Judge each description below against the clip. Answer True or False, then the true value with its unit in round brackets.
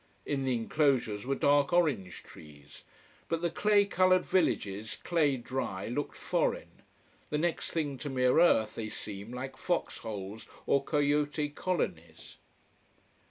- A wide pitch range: True (6.3 semitones)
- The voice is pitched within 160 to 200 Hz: False (135 Hz)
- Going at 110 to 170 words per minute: True (135 wpm)